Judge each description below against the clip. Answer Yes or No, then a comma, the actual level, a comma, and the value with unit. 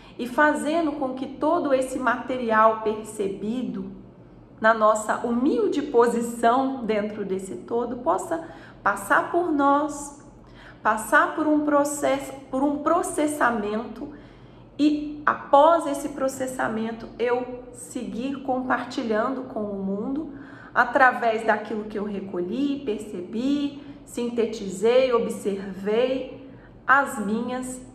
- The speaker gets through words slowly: Yes, slow, 100 wpm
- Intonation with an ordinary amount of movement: Yes, average, 4.5 semitones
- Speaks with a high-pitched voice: Yes, very high, 250 Hz